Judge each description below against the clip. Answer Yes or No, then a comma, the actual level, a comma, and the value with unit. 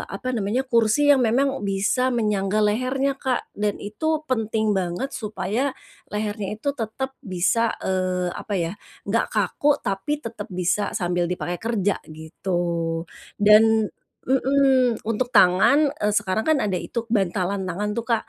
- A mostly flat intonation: No, average, 3.6 semitones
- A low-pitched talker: No, high, 210 Hz